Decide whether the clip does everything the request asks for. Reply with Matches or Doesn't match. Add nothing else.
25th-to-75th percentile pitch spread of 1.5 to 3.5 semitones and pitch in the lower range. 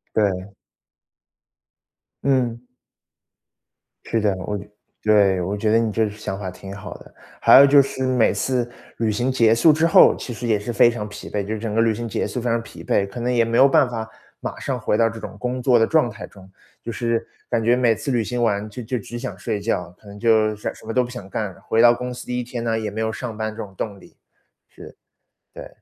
Matches